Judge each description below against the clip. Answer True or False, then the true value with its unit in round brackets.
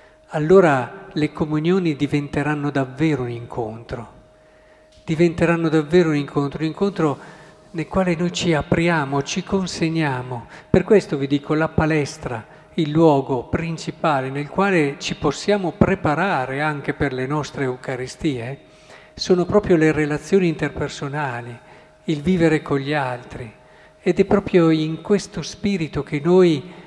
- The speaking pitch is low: False (155 Hz)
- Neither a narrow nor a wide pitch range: True (3.4 semitones)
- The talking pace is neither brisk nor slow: True (125 wpm)